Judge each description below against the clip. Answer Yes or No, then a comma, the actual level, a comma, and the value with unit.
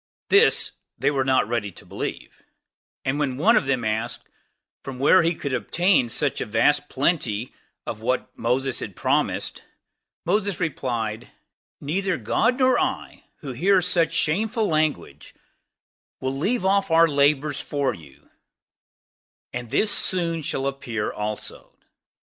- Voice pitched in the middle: Yes, medium, 145 Hz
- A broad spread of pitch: Yes, wide, 5.9 semitones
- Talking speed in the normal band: No, slow, 125 wpm